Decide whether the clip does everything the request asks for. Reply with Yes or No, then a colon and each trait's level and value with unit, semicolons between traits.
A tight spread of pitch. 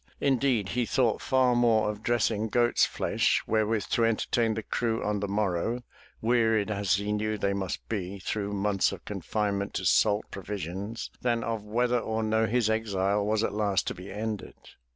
Yes: narrow, 2.1 semitones